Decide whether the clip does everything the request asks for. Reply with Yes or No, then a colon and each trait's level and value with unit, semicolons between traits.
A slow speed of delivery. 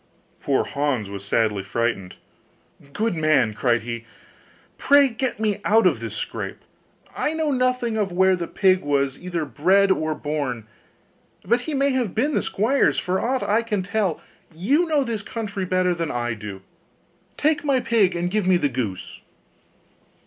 No: average, 165 wpm